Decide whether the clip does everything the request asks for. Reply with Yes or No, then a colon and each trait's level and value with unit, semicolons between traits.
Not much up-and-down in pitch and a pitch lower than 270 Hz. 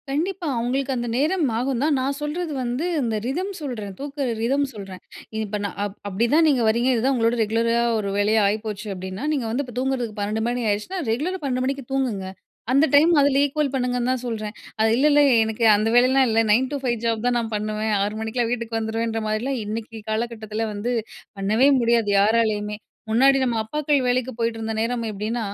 No: average, 3.6 semitones; high, 235 Hz